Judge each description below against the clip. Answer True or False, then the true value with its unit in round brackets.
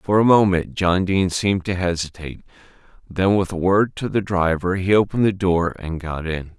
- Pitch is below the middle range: True (90 Hz)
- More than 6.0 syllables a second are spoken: False (5.3 syllables/s)